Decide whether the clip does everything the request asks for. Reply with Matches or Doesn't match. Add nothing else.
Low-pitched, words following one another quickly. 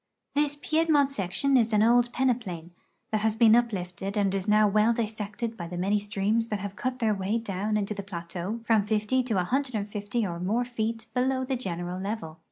Doesn't match